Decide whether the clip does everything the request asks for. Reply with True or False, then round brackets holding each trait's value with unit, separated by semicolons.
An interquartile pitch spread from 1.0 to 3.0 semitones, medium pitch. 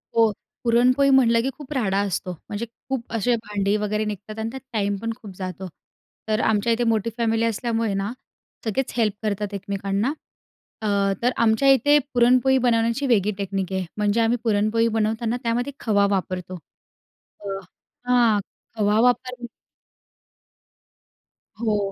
False (2.7 semitones; 225 Hz)